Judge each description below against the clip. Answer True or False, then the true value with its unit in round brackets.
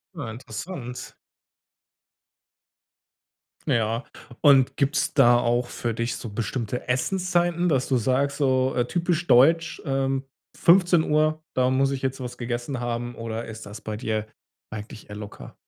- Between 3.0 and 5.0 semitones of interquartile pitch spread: True (3.7 semitones)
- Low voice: True (130 Hz)